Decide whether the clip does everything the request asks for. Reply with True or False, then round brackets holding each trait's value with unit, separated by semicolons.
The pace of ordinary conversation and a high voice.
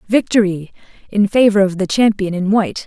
True (165 wpm; 200 Hz)